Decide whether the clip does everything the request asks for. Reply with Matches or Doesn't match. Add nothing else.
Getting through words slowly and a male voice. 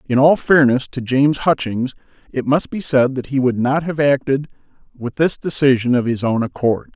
Doesn't match